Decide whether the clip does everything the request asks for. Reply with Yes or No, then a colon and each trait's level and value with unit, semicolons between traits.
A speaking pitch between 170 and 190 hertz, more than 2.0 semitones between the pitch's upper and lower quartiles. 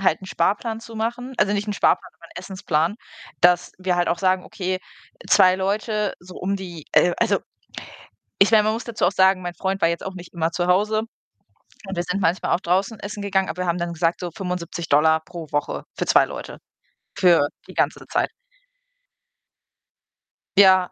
Yes: medium, 185 Hz; narrow, 2.4 semitones